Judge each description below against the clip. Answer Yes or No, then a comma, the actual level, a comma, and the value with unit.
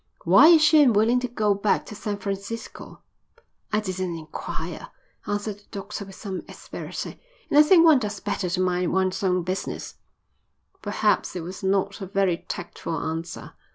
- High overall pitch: Yes, high, 200 Hz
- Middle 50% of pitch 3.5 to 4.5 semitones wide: No, narrow, 2.6 semitones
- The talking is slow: No, average, 165 wpm